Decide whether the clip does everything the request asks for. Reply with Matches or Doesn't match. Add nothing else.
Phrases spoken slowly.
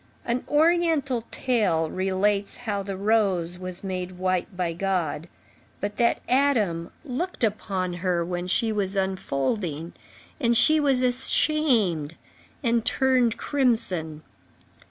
Matches